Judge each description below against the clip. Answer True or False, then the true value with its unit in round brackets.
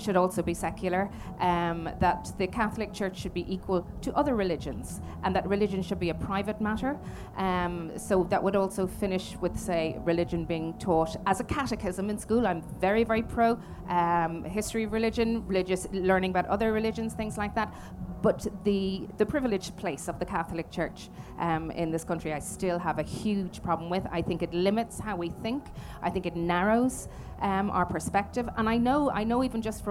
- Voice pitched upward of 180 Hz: True (190 Hz)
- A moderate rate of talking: True (195 wpm)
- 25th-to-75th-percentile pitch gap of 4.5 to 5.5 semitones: False (3.5 semitones)